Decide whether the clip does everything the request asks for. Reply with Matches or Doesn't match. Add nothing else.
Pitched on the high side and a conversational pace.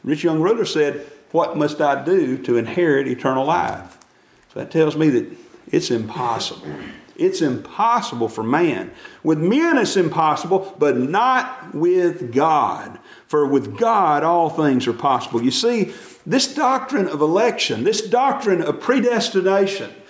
Matches